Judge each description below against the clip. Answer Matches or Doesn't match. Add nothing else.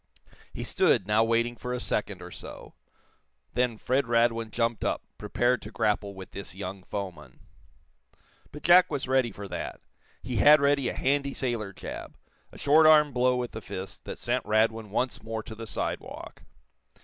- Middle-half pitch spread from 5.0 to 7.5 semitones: Doesn't match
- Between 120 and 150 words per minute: Doesn't match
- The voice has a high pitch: Doesn't match